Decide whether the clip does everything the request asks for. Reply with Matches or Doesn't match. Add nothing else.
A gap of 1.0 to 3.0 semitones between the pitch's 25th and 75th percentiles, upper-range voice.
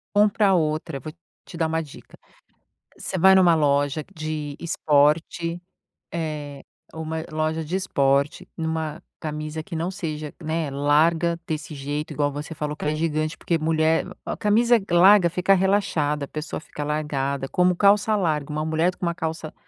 Doesn't match